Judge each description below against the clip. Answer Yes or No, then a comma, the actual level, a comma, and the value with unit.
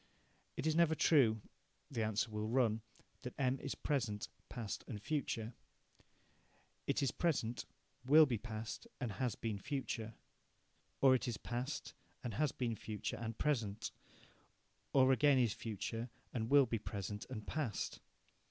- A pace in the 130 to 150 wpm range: Yes, average, 145 wpm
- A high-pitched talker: No, low, 120 Hz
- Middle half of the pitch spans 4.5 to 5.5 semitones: No, average, 3.8 semitones